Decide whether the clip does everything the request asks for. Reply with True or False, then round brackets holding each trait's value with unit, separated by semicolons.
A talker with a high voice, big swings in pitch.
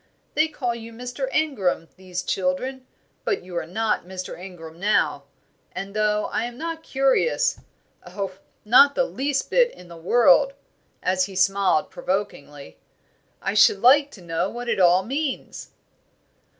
True (210 Hz; 6.5 semitones)